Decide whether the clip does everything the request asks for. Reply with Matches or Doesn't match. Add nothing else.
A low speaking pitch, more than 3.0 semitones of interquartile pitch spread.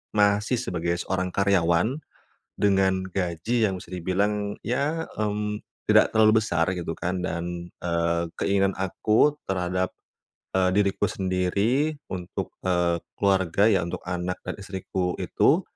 Doesn't match